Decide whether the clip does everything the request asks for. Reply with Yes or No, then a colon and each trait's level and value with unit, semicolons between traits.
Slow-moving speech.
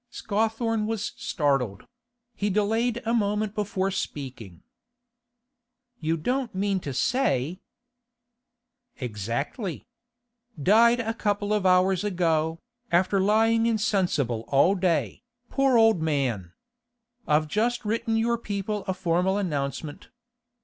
Yes: slow, 110 wpm